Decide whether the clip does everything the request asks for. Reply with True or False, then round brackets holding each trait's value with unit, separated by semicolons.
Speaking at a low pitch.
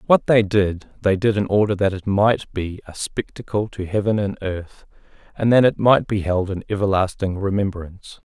True (100 Hz)